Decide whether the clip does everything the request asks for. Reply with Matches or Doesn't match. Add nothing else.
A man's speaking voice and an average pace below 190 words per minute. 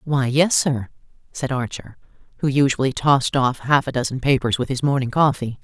Doesn't match